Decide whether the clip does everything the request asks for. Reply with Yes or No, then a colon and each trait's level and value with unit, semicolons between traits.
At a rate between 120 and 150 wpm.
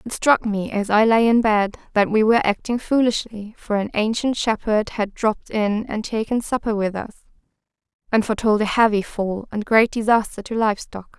No: average, 195 wpm